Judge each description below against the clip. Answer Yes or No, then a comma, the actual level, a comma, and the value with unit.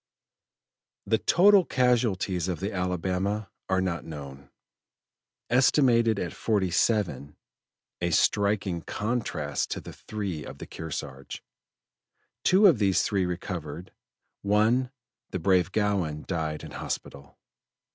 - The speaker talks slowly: Yes, slow, 115 wpm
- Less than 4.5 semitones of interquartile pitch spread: No, average, 4.8 semitones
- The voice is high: No, very low, 95 Hz